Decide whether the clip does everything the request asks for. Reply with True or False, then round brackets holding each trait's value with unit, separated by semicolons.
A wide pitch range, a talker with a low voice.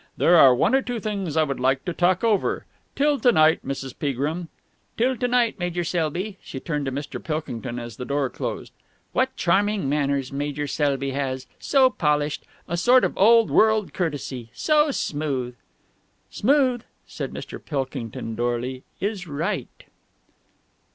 False (7.6 semitones; 155 Hz)